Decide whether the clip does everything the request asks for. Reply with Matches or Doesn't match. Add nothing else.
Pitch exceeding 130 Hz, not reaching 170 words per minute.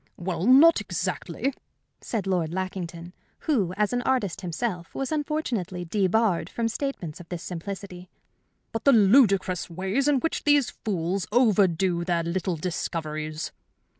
Matches